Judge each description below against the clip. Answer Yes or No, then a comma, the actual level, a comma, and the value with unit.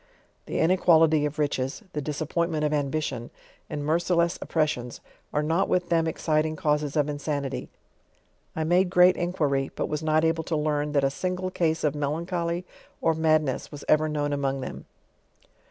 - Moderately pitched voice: Yes, medium, 155 Hz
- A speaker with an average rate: Yes, average, 165 wpm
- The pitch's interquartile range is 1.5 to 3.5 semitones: Yes, narrow, 2.4 semitones